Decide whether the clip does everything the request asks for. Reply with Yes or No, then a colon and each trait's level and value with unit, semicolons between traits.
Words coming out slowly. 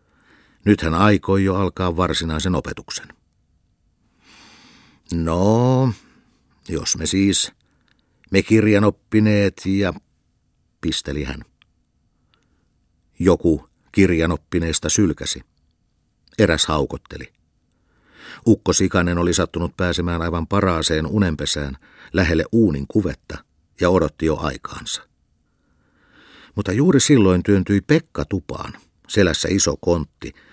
Yes: slow, 90 wpm